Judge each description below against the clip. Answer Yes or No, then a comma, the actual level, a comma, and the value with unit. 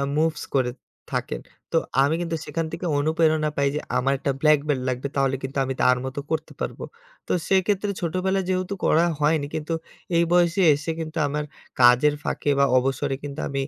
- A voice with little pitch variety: No, average, 3.2 semitones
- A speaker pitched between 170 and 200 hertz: No, medium, 150 Hz